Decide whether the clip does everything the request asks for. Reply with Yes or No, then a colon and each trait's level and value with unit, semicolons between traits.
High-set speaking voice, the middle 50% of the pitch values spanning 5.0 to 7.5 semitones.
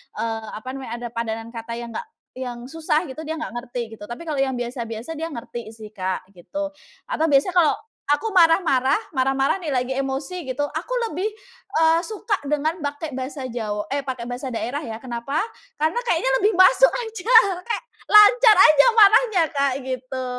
Yes: very high, 275 Hz; wide, 5.4 semitones